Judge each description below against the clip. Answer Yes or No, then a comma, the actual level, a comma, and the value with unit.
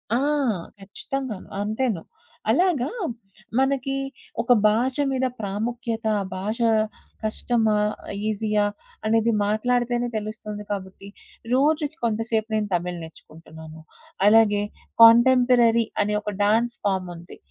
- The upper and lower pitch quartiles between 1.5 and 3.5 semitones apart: Yes, average, 2.8 semitones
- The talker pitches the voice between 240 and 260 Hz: No, high, 225 Hz